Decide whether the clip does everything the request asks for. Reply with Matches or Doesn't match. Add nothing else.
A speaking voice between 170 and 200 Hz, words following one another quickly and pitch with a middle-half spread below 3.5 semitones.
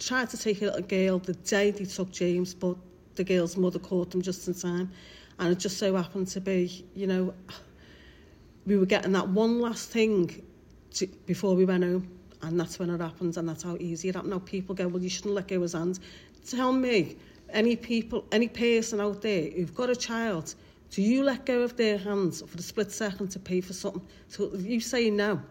Matches